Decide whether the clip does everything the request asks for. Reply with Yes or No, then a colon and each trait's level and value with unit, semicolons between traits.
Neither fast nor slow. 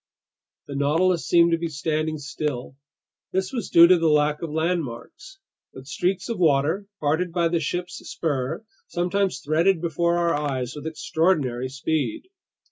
Yes: average, 150 wpm